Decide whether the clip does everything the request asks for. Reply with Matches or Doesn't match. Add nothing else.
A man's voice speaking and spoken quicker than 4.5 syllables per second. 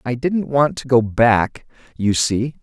Doesn't match